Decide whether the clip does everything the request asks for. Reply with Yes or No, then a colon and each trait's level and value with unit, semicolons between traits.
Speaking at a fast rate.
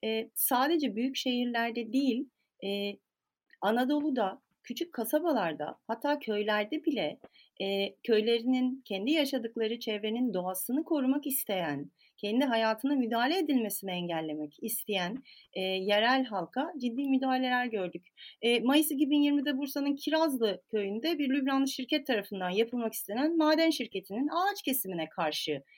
No: average, 115 wpm